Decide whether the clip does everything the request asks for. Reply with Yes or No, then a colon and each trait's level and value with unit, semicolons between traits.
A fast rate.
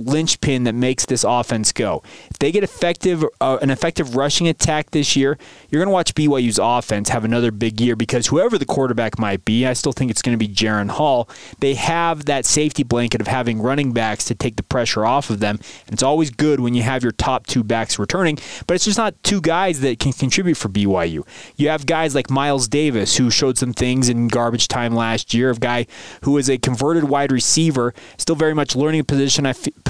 Yes: fast, 225 wpm